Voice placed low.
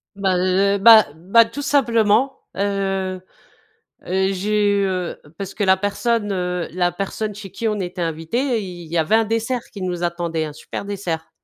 No: high, 195 Hz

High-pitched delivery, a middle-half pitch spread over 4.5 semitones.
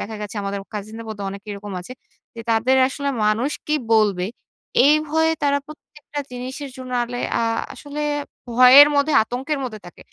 Yes: high, 245 Hz; average, 5.1 semitones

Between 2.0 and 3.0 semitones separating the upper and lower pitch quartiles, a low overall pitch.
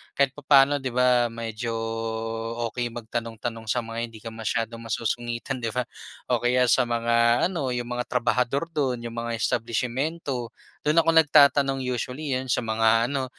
Yes: narrow, 2.5 semitones; low, 120 Hz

